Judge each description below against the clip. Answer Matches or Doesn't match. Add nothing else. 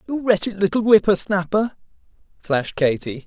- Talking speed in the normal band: Doesn't match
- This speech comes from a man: Matches